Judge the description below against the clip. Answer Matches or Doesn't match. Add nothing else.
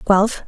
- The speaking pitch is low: Doesn't match